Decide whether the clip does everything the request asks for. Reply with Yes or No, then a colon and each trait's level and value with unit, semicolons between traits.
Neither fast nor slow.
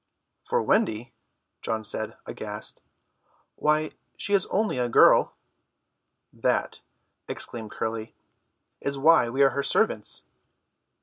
No: slow, 110 wpm